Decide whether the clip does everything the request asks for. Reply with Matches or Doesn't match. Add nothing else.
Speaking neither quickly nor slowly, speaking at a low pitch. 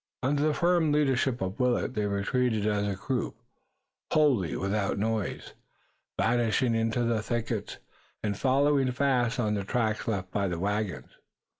Matches